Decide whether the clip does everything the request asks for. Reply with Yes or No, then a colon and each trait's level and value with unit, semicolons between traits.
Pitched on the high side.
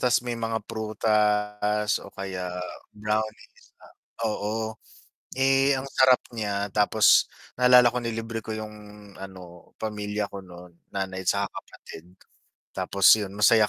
No: low, 105 Hz